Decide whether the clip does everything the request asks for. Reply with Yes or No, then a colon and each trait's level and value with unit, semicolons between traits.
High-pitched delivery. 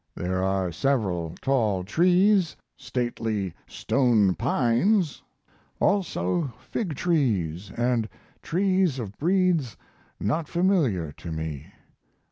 No: low, 125 Hz